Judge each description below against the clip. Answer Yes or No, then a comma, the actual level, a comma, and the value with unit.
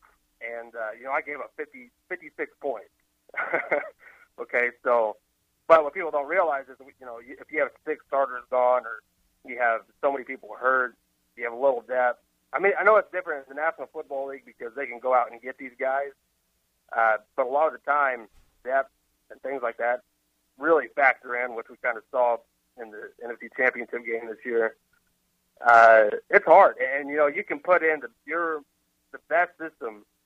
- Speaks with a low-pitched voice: Yes, low, 130 Hz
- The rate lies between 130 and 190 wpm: No, average, 200 wpm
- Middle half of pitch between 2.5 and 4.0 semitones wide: No, average, 4.6 semitones